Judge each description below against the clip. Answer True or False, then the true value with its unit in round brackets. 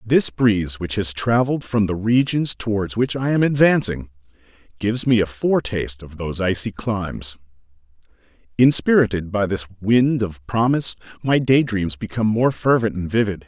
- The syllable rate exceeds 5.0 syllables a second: True (5.2 syllables/s)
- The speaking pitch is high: False (105 Hz)